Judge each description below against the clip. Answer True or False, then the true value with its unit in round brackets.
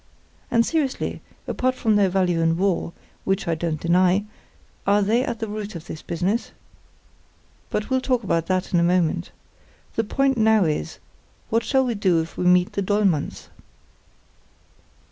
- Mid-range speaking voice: False (195 Hz)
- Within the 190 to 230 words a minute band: False (165 wpm)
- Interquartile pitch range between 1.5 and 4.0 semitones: False (4.5 semitones)